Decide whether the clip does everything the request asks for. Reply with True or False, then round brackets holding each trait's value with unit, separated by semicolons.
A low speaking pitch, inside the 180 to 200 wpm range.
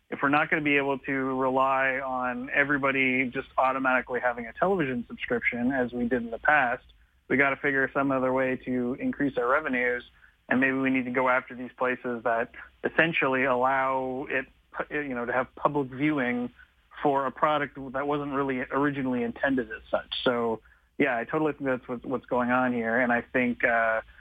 True (130 Hz; 190 wpm)